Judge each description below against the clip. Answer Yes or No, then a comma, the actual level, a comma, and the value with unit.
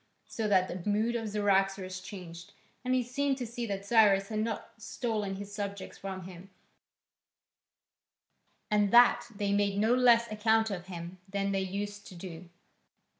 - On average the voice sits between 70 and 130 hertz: No, high, 205 Hz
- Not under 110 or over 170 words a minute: Yes, average, 160 wpm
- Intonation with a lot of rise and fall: No, narrow, 2.6 semitones